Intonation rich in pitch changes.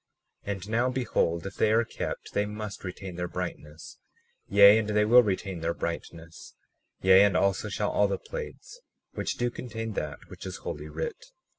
No: average, 3.8 semitones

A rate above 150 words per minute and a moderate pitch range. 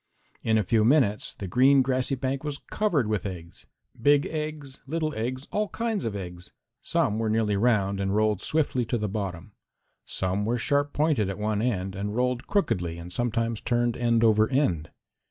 Yes: average, 180 wpm; average, 4.9 semitones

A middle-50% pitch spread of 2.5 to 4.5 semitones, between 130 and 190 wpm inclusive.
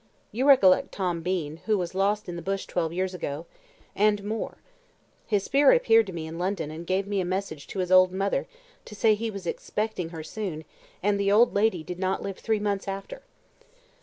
No: average, 2.8 semitones; fast, 205 wpm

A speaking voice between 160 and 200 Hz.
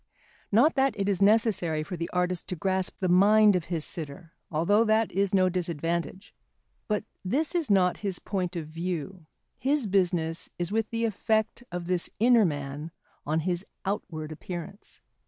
Yes: medium, 185 Hz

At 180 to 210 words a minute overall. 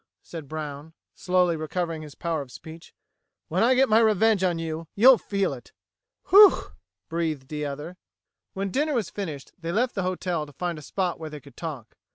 Yes: average, 190 wpm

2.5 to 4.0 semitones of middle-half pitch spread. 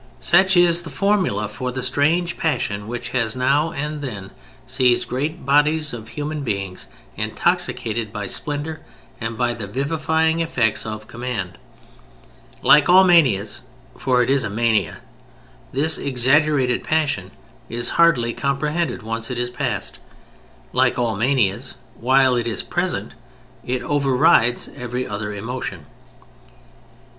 No: average, 4.7 semitones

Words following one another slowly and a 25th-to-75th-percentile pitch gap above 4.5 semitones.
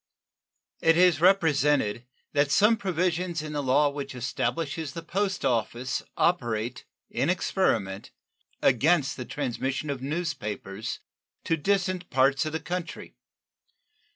Yes: slow, 125 wpm; average, 5.2 semitones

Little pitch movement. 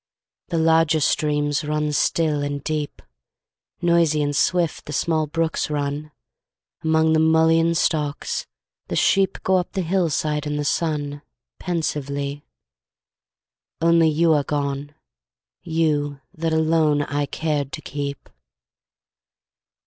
Yes: narrow, 2.0 semitones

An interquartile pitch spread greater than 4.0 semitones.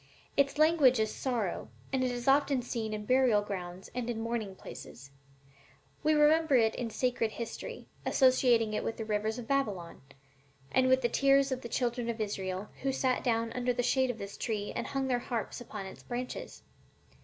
No: average, 3.2 semitones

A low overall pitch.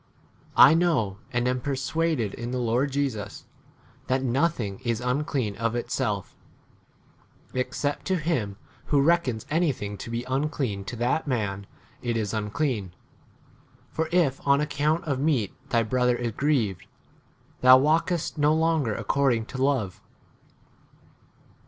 Yes: low, 130 Hz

